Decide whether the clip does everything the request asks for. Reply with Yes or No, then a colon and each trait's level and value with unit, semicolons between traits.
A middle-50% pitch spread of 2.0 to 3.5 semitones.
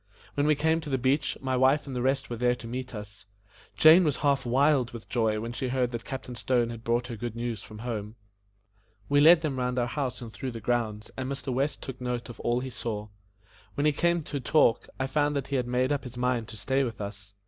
Yes: average, 2.9 semitones